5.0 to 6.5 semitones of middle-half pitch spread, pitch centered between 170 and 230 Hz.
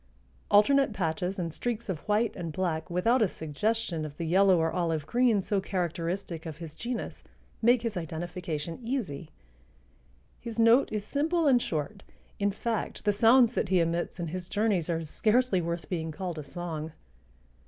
Yes: wide, 5.5 semitones; medium, 185 Hz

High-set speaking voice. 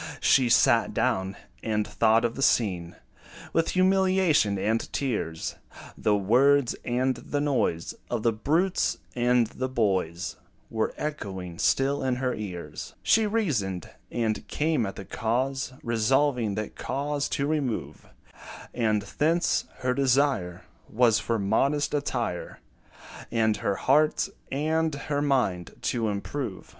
No: low, 120 Hz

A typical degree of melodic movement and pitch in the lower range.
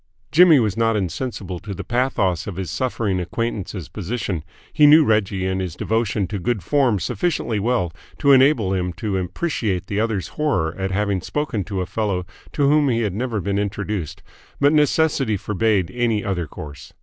Yes: average, 4.6 semitones; low, 105 Hz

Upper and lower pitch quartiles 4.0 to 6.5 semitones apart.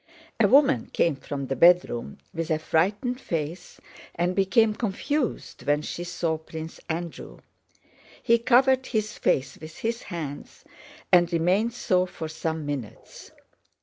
Yes: wide, 5.6 semitones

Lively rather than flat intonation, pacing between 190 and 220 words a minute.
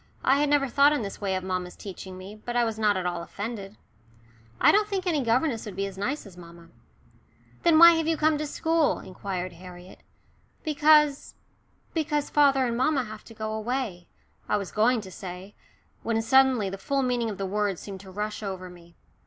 Yes: wide, 6.7 semitones; average, 200 wpm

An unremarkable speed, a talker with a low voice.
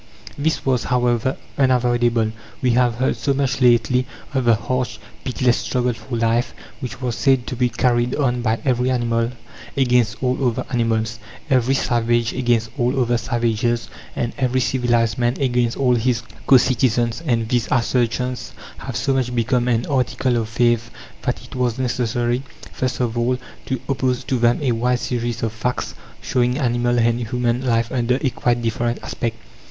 Yes: average, 170 wpm; low, 120 Hz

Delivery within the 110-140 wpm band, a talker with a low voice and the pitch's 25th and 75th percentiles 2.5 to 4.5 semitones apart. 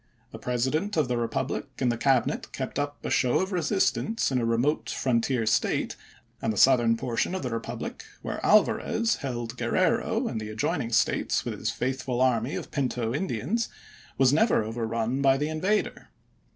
No: average, 175 wpm; low, 130 Hz; average, 4.2 semitones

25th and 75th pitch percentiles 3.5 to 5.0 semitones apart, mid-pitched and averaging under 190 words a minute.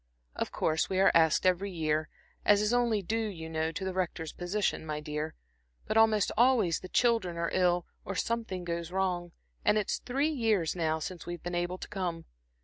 No: average, 4.1 semitones; medium, 180 Hz; average, 195 wpm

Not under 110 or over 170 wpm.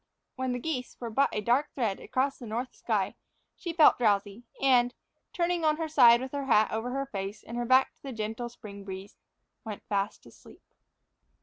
No: average, 195 wpm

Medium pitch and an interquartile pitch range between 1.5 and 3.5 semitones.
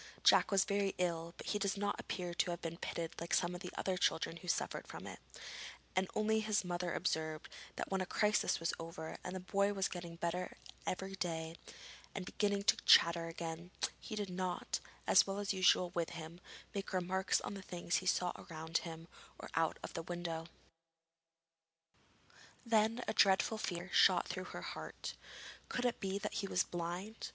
Yes: medium, 180 Hz; average, 2.8 semitones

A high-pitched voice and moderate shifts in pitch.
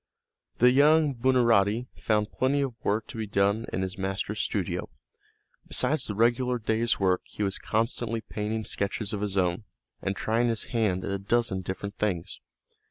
No: low, 110 Hz; average, 3.3 semitones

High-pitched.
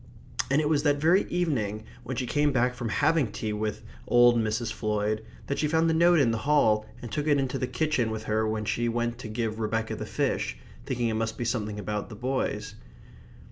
No: low, 120 Hz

